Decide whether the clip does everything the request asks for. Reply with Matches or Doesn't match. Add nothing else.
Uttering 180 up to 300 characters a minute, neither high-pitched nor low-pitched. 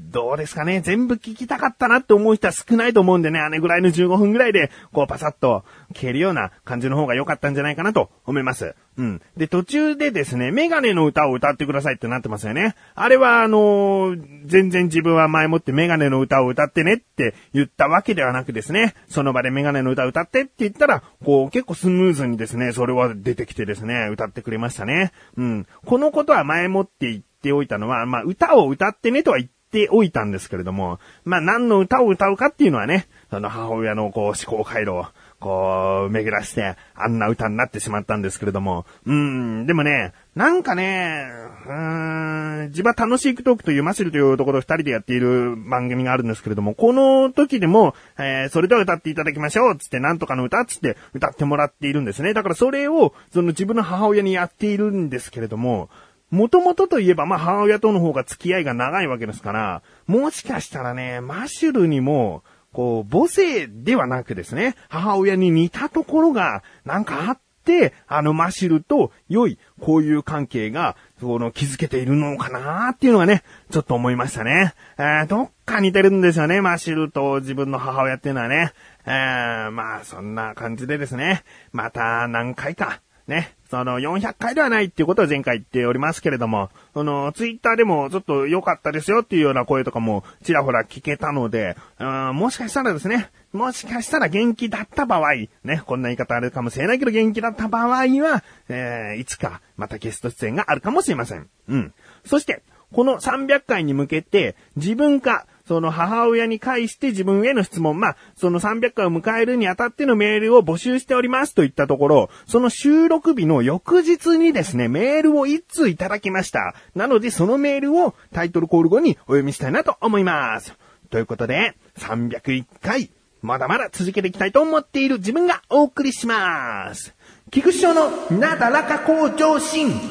Doesn't match